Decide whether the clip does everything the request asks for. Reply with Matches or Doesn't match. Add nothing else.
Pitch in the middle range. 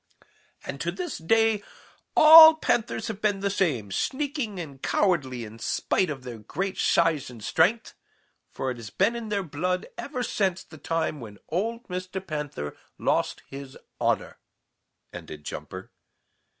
Matches